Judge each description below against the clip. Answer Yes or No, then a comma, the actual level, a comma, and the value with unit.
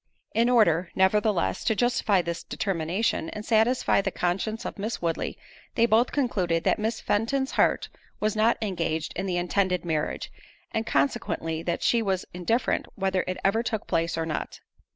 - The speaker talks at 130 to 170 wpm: Yes, average, 165 wpm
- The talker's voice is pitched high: Yes, high, 195 Hz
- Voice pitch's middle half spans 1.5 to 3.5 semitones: No, average, 4.6 semitones